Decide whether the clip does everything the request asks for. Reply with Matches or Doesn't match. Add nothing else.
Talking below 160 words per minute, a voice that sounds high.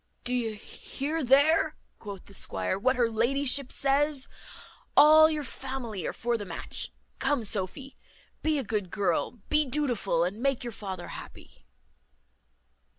Matches